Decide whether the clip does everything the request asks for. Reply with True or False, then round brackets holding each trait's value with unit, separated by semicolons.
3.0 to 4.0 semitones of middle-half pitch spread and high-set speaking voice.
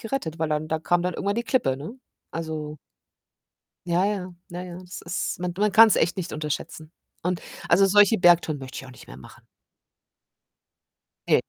False (3.6 semitones; 175 Hz)